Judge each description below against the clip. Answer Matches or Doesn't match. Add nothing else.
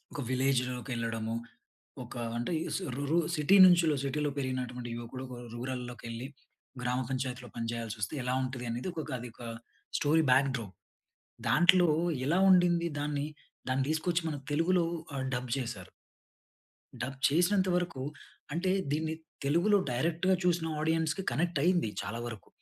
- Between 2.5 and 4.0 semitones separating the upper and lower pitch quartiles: Doesn't match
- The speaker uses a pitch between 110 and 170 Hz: Matches